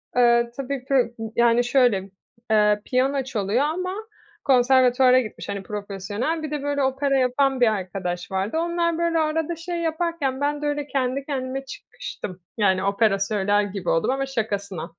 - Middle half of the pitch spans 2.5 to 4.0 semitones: No, wide, 5.5 semitones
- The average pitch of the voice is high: Yes, very high, 255 Hz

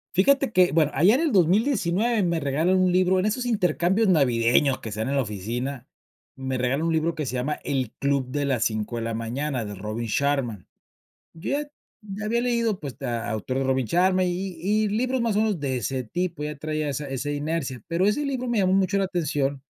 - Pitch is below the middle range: No, medium, 155 Hz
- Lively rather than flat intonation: Yes, wide, 6.6 semitones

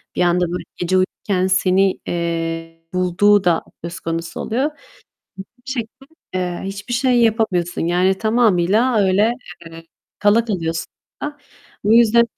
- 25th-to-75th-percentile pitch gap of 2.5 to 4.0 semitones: No, average, 4.4 semitones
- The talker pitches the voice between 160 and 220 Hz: Yes, high, 190 Hz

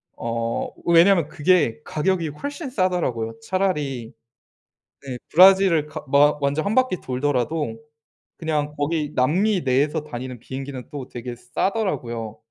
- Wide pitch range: Yes, wide, 6.2 semitones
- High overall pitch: No, medium, 150 Hz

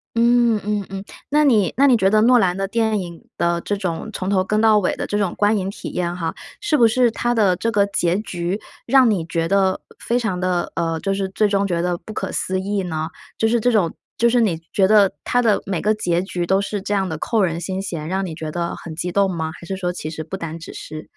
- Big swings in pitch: No, average, 3.7 semitones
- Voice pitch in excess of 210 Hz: No, high, 195 Hz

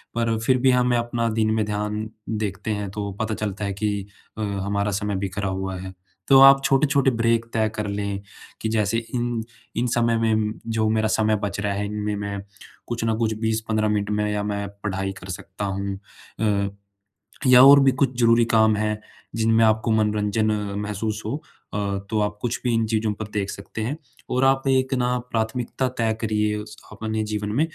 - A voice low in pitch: Yes, low, 110 Hz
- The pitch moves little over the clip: Yes, narrow, 1.9 semitones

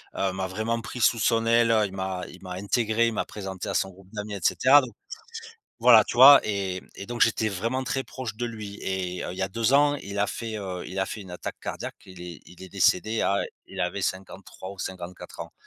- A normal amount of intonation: Yes, average, 3.6 semitones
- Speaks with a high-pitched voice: No, low, 100 Hz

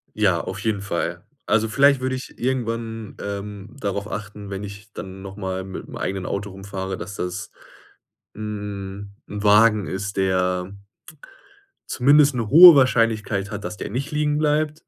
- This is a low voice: Yes, low, 105 Hz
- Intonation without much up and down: No, average, 3.0 semitones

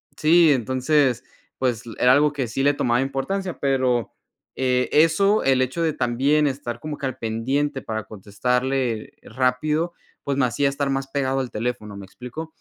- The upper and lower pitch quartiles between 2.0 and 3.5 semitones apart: Yes, average, 2.9 semitones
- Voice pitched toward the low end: Yes, low, 130 Hz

